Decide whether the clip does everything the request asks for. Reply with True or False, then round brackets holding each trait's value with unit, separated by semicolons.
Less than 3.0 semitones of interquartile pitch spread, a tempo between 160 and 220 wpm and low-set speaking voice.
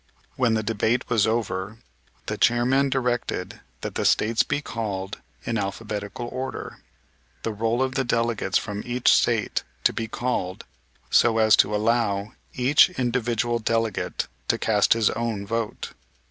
False (2.4 semitones; 140 wpm; 115 Hz)